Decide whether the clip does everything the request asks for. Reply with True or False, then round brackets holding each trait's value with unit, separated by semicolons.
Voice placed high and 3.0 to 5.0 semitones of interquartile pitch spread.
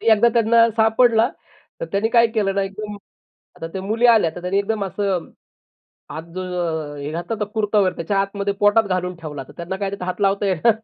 True (200 Hz; 3.5 semitones)